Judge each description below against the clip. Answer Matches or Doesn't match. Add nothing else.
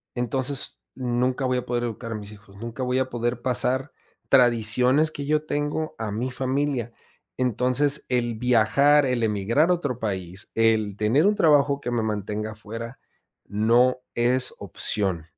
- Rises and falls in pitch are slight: Doesn't match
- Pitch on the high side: Doesn't match